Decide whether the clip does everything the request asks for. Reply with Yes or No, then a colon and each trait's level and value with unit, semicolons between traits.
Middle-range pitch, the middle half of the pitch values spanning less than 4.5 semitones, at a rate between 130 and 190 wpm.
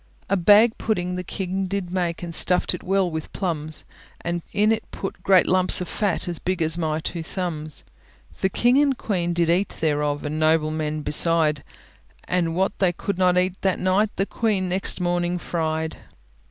Yes: medium, 180 Hz; average, 2.9 semitones; average, 180 wpm